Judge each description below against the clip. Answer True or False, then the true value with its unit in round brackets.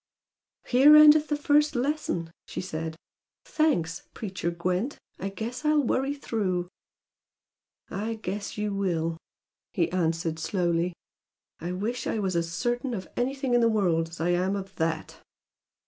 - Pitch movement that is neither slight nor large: False (6.3 semitones)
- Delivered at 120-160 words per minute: True (145 wpm)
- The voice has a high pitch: True (195 Hz)